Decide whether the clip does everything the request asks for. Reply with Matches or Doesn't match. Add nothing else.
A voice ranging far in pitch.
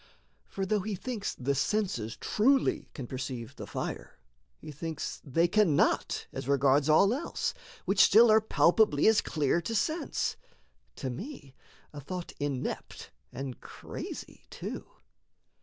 Matches